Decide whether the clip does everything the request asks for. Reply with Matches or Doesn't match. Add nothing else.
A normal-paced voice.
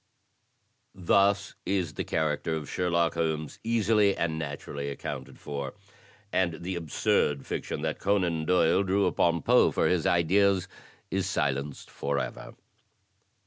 Doesn't match